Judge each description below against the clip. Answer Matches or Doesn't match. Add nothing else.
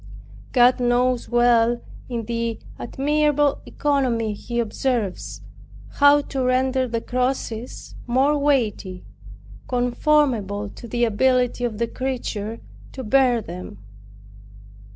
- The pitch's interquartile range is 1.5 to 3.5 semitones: Matches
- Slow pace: Matches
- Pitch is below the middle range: Doesn't match